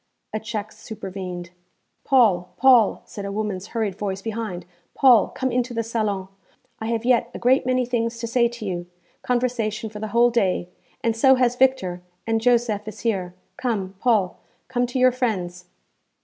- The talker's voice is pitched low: No, high, 225 Hz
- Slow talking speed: No, average, 170 wpm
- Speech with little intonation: No, average, 3.6 semitones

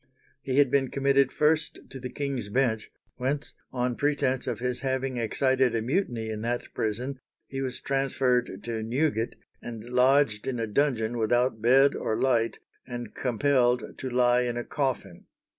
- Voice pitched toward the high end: No, low, 125 Hz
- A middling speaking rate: Yes, average, 160 wpm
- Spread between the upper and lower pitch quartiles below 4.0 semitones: Yes, narrow, 2.4 semitones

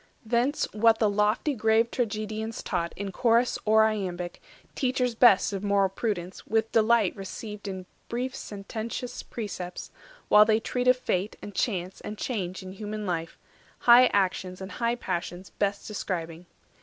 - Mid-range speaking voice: No, high, 210 Hz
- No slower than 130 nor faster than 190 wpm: Yes, average, 155 wpm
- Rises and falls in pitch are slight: No, average, 3.3 semitones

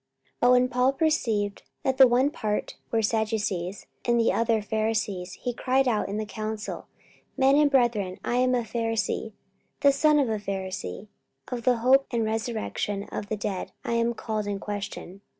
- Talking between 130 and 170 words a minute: No, average, 180 wpm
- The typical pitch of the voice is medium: No, high, 225 Hz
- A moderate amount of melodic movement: Yes, average, 3.2 semitones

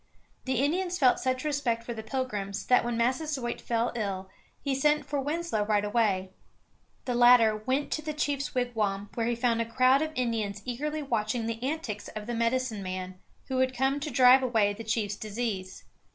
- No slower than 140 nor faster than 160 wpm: No, average, 185 wpm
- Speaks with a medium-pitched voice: No, high, 240 Hz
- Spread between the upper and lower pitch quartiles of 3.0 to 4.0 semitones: Yes, average, 3.7 semitones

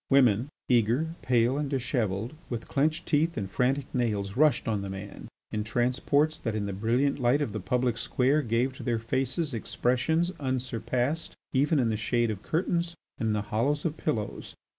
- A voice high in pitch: No, low, 125 Hz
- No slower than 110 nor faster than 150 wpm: No, average, 180 wpm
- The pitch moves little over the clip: No, average, 4.3 semitones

